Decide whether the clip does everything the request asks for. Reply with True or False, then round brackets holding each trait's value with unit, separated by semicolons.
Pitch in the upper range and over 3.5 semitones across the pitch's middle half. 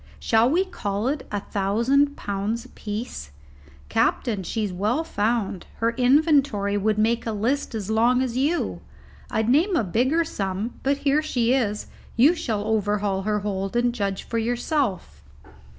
True (230 Hz; 4.4 semitones)